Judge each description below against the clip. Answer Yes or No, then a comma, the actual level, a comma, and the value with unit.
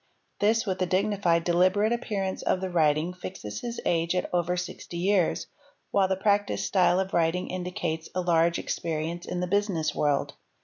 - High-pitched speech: No, medium, 180 Hz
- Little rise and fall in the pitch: Yes, narrow, 2.3 semitones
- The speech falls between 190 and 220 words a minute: No, average, 170 wpm